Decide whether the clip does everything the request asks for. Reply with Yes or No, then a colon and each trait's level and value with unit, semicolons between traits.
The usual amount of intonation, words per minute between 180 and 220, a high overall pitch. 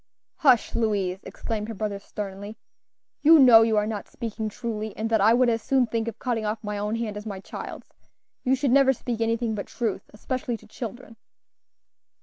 No: narrow, 2.2 semitones; average, 190 wpm; high, 225 Hz